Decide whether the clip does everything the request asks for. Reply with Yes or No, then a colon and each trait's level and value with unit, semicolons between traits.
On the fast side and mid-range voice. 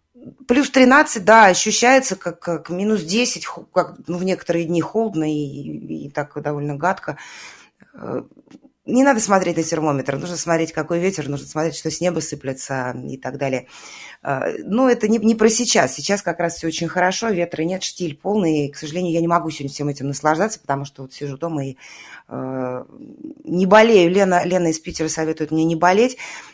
Yes: fast, 185 wpm; medium, 170 Hz